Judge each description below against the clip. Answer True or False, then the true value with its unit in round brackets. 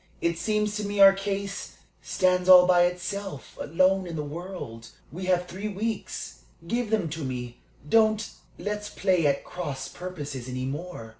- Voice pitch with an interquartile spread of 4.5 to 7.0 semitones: True (4.9 semitones)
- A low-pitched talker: False (180 Hz)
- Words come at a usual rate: True (160 wpm)